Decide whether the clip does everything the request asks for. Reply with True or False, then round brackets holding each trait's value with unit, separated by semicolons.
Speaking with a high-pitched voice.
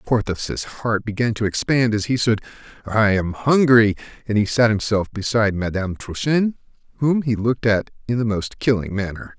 False (110 Hz)